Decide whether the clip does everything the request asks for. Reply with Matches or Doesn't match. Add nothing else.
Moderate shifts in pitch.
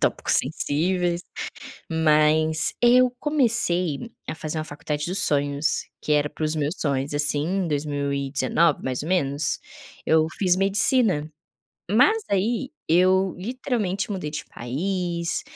Matches